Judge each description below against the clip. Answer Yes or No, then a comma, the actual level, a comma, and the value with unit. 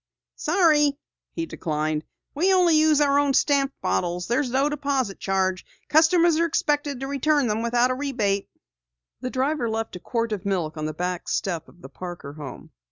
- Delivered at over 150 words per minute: Yes, average, 170 wpm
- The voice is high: Yes, very high, 255 Hz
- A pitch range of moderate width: No, wide, 7.9 semitones